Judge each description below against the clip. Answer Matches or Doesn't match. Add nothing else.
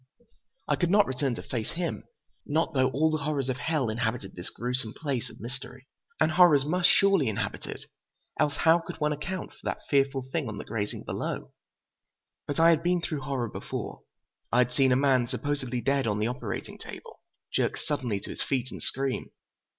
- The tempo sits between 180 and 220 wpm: Matches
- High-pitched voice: Doesn't match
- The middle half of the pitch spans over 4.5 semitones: Doesn't match